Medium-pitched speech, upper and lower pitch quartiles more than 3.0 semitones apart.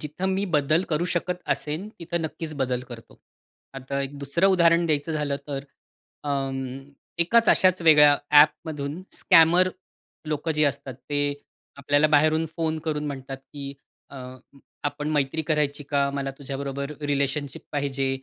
No: medium, 150 Hz; narrow, 2.5 semitones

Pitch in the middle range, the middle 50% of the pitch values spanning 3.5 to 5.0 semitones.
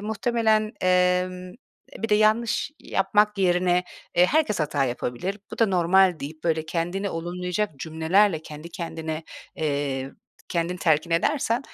Yes: medium, 180 Hz; average, 4.2 semitones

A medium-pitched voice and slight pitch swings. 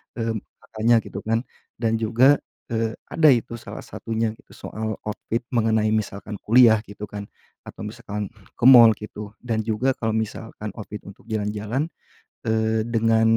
No: low, 110 Hz; narrow, 1.3 semitones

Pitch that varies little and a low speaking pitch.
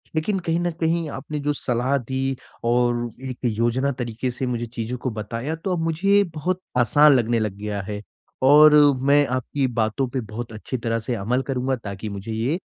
No: average, 4.3 semitones; low, 130 Hz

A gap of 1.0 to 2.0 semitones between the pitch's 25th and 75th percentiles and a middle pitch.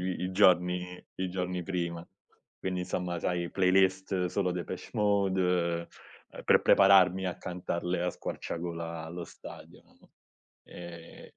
No: narrow, 1.3 semitones; very low, 90 Hz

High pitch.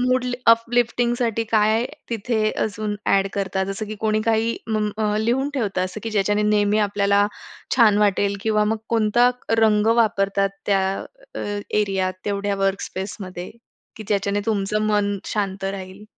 Yes: high, 210 Hz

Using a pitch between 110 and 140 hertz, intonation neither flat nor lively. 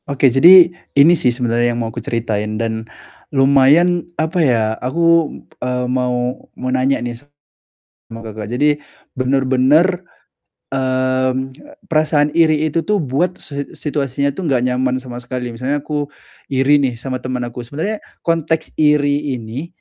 Yes: low, 135 Hz; average, 3.5 semitones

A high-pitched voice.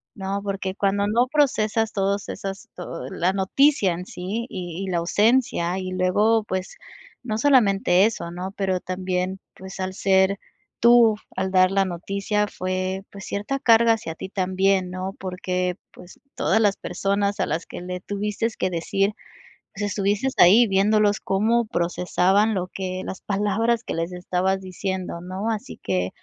Yes: high, 195 Hz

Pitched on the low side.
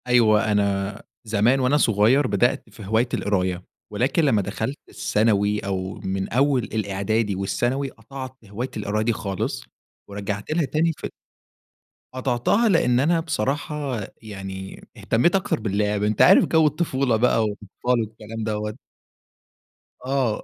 Yes: low, 110 Hz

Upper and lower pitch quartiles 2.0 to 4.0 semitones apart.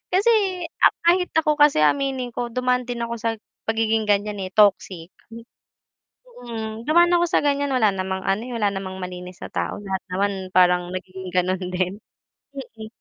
No: average, 5.0 semitones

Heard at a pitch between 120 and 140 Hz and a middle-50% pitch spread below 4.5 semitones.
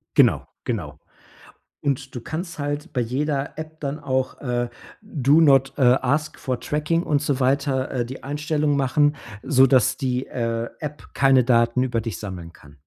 Yes: low, 135 Hz; average, 2.9 semitones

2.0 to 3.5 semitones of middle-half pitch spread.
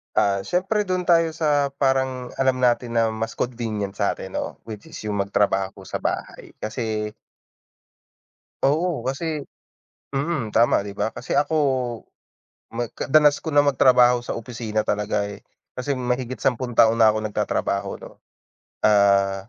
No: average, 4.8 semitones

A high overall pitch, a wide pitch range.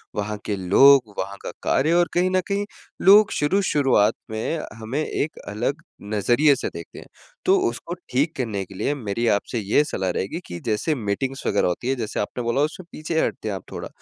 No: low, 125 Hz; wide, 6.9 semitones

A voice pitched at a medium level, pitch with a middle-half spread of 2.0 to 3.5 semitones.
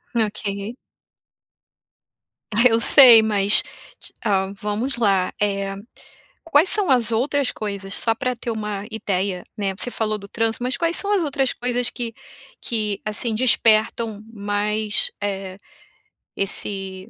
No: high, 215 Hz; average, 3.2 semitones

